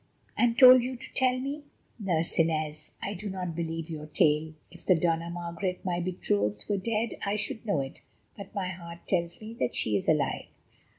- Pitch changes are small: No, average, 4.6 semitones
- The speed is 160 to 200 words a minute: Yes, average, 190 wpm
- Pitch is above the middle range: No, medium, 175 Hz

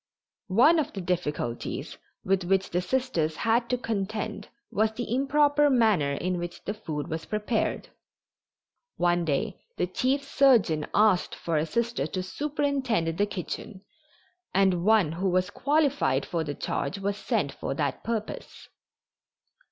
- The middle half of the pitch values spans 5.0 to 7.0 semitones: Yes, wide, 5.5 semitones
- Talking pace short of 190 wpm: Yes, average, 145 wpm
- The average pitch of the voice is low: No, high, 200 Hz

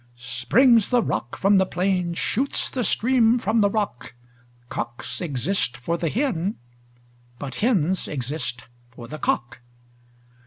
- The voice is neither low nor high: Yes, medium, 180 Hz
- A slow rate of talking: Yes, slow, 130 wpm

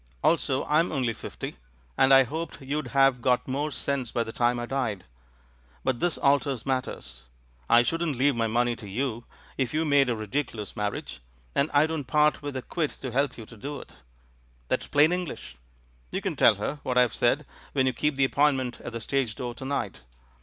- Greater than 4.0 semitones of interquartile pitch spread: No, average, 3.2 semitones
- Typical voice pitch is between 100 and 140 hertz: Yes, low, 135 Hz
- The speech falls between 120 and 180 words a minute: No, average, 200 wpm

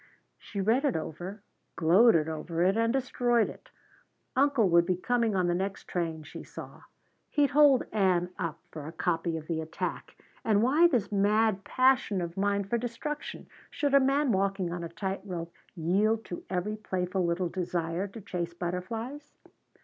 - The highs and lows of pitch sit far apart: No, average, 5.0 semitones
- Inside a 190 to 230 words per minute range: No, average, 170 wpm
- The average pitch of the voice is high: Yes, high, 195 Hz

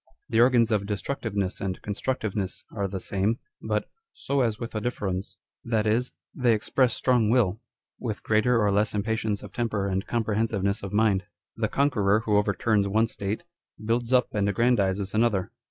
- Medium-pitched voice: No, low, 110 Hz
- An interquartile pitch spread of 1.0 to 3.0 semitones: Yes, narrow, 2.6 semitones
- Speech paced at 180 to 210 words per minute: Yes, average, 185 wpm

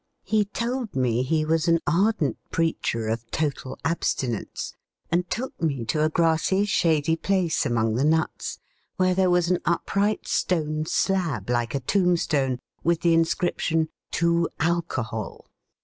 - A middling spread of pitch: Yes, average, 4.4 semitones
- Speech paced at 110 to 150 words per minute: Yes, average, 140 wpm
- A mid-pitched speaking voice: Yes, medium, 165 Hz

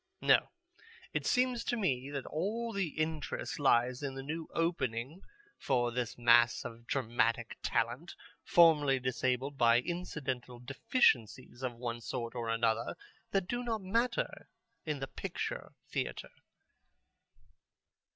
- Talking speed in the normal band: No, slow, 125 wpm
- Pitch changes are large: Yes, wide, 5.9 semitones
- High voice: No, low, 135 Hz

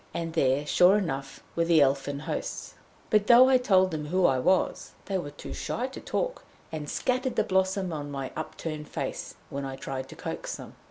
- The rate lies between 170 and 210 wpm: Yes, average, 200 wpm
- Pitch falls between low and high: Yes, medium, 165 Hz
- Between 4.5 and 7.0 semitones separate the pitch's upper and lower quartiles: Yes, average, 5.2 semitones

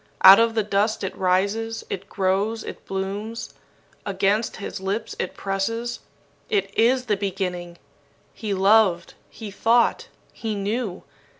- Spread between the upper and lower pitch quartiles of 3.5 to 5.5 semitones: No, average, 2.7 semitones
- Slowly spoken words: Yes, slow, 130 wpm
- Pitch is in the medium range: No, high, 205 Hz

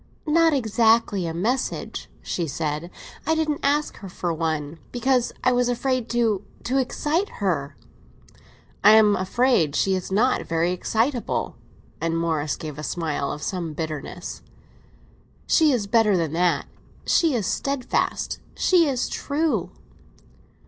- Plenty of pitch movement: Yes, wide, 7.4 semitones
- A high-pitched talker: Yes, high, 210 Hz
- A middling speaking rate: No, slow, 130 wpm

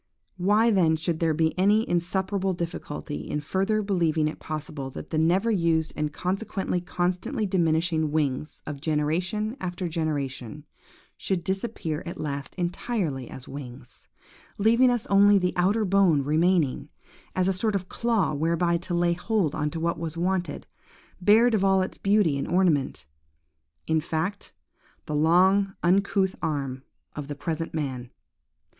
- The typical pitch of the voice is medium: Yes, medium, 170 Hz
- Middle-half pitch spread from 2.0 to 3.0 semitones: No, average, 4.1 semitones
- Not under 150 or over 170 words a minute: No, average, 140 wpm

